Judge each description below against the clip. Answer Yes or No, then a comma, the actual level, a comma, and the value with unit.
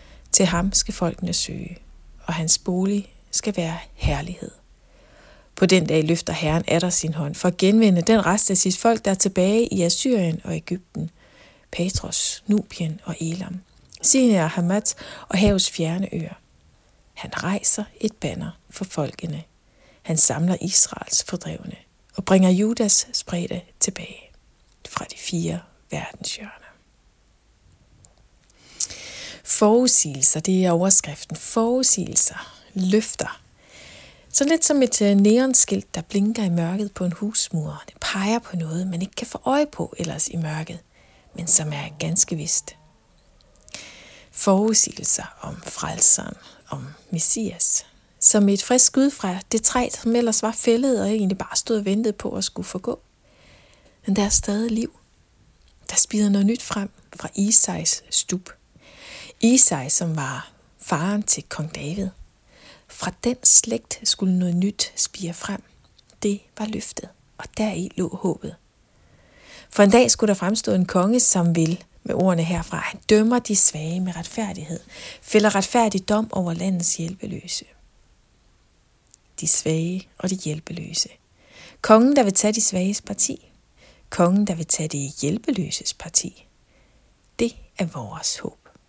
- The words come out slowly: Yes, slow, 140 wpm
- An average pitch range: Yes, average, 4.1 semitones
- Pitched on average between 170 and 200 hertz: Yes, high, 190 Hz